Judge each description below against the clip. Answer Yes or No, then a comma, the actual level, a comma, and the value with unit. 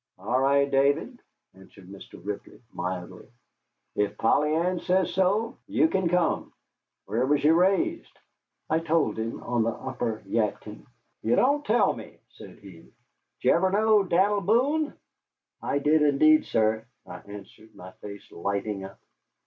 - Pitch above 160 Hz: No, medium, 145 Hz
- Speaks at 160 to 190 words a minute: No, average, 150 wpm